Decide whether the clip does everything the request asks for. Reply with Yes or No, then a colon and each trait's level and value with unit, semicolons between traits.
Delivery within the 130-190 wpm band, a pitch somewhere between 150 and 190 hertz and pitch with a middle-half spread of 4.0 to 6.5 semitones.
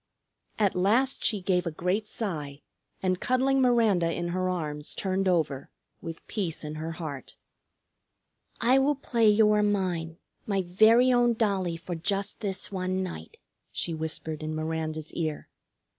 Yes: average, 150 wpm; medium, 185 Hz; average, 4.6 semitones